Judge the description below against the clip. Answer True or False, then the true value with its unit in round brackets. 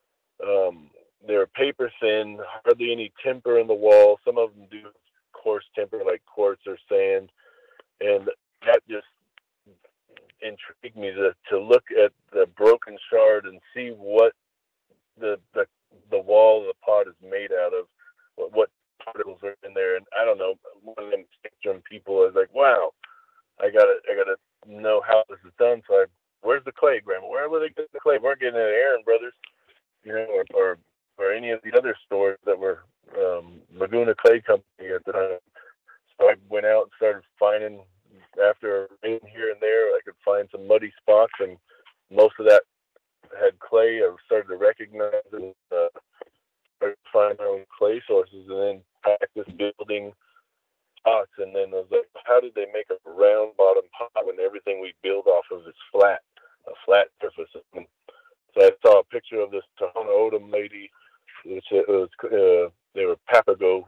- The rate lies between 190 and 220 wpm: False (180 wpm)